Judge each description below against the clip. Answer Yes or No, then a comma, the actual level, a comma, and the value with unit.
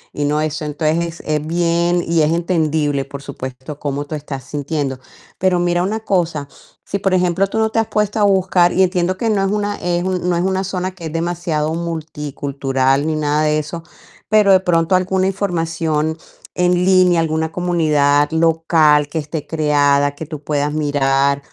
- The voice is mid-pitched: Yes, medium, 165 Hz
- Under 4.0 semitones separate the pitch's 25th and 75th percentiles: Yes, average, 3.4 semitones